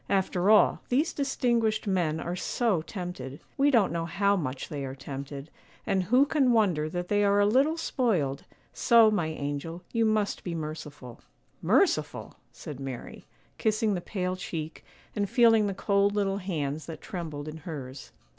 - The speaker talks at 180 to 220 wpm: No, average, 165 wpm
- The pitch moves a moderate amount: No, wide, 5.9 semitones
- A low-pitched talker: No, medium, 185 Hz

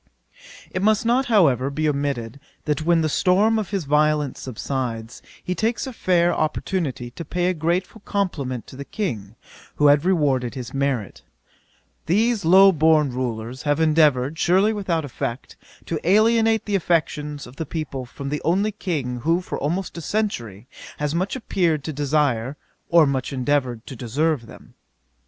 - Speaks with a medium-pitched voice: Yes, medium, 155 Hz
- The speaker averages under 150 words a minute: No, average, 160 wpm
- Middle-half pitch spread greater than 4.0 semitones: Yes, wide, 5.5 semitones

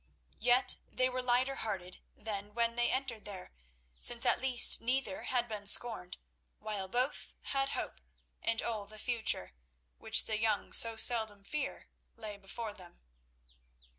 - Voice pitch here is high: Yes, high, 225 Hz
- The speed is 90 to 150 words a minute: Yes, average, 145 wpm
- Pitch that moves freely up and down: No, average, 3.1 semitones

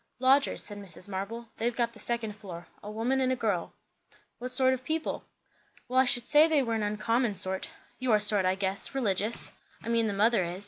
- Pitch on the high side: Yes, high, 225 Hz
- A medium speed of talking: No, fast, 210 wpm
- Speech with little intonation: No, average, 3.9 semitones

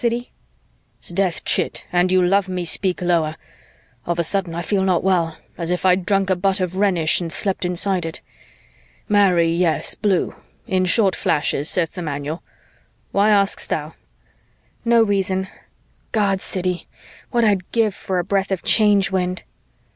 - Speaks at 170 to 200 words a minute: No, average, 160 wpm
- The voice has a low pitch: No, medium, 185 Hz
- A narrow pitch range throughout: Yes, narrow, 2.3 semitones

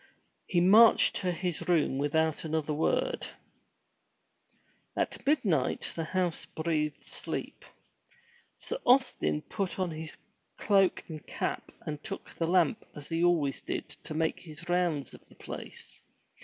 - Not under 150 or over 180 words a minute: No, slow, 135 wpm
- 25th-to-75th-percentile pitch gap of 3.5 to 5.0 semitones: No, average, 3.1 semitones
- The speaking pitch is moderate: Yes, medium, 165 Hz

